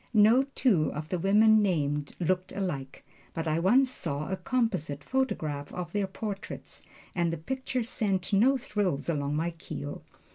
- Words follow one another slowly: No, average, 155 wpm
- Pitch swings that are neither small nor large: No, wide, 5.9 semitones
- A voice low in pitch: No, medium, 185 Hz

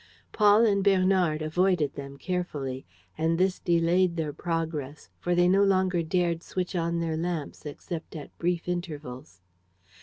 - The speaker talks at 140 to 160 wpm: Yes, average, 145 wpm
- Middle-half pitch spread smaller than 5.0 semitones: Yes, average, 2.8 semitones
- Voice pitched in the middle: Yes, medium, 170 Hz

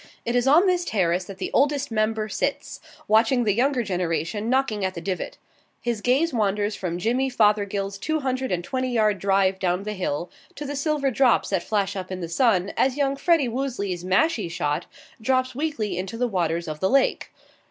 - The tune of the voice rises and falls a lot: Yes, wide, 5.7 semitones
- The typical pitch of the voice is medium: No, high, 215 Hz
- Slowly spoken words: No, average, 195 wpm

